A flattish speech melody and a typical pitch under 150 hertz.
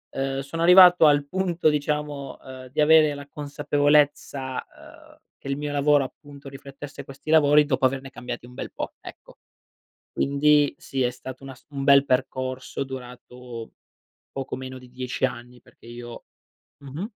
Yes: narrow, 2.2 semitones; medium, 140 Hz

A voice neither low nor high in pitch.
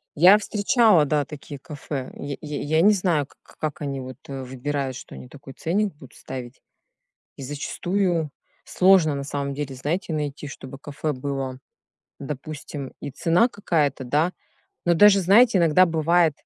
Yes: medium, 150 Hz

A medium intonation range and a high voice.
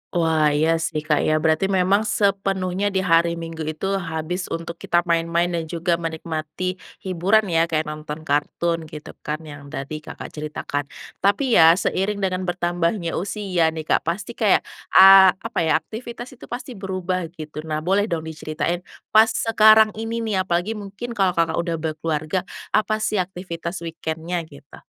No: average, 3.3 semitones; medium, 170 Hz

